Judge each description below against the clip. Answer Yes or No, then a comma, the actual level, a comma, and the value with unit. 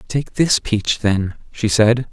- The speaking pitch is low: Yes, low, 115 Hz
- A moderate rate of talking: Yes, average, 170 wpm